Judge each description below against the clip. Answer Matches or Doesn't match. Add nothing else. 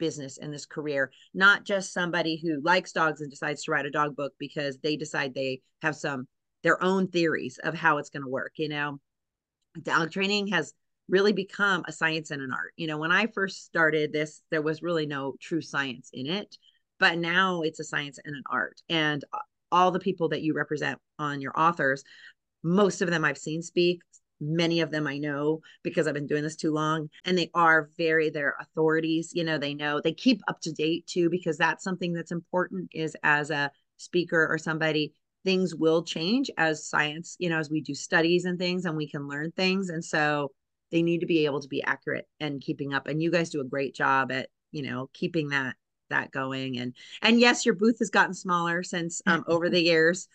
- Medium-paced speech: Doesn't match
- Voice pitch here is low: Doesn't match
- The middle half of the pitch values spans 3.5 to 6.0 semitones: Doesn't match